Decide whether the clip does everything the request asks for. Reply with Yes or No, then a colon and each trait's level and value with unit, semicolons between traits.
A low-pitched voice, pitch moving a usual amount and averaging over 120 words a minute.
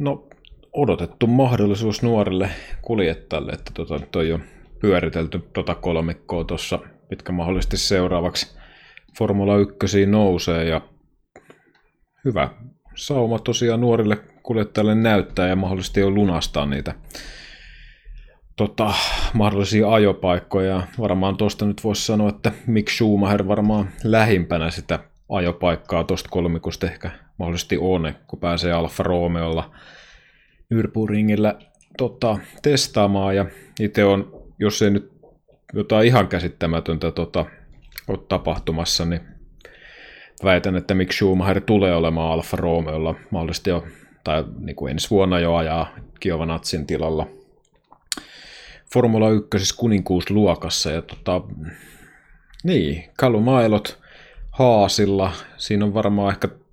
No: very low, 95 Hz; average, 3.7 semitones; average, 110 wpm